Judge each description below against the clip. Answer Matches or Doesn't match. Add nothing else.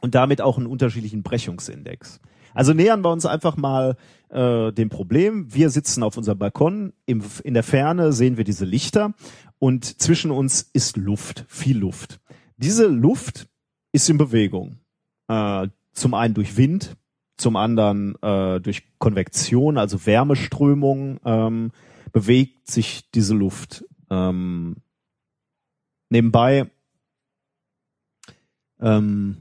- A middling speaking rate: Doesn't match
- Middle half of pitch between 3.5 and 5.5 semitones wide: Matches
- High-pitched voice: Doesn't match